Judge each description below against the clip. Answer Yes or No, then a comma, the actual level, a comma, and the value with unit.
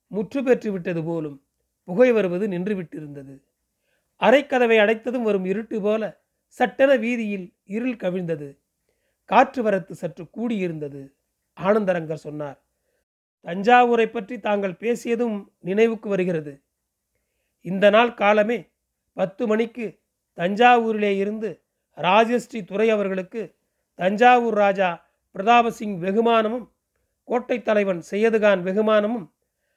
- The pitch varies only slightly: No, average, 4.0 semitones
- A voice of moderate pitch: No, high, 210 Hz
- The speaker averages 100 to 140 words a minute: No, average, 90 wpm